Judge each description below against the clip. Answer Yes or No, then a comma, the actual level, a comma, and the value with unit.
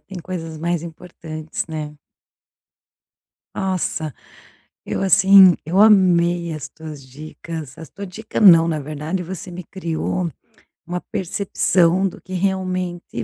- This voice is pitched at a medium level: Yes, medium, 175 Hz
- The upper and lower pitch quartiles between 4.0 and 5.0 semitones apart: No, average, 2.8 semitones